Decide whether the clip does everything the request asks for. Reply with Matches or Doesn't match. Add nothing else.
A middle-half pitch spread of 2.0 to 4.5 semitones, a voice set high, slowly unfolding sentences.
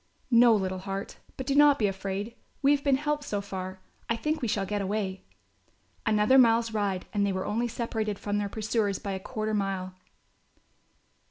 Doesn't match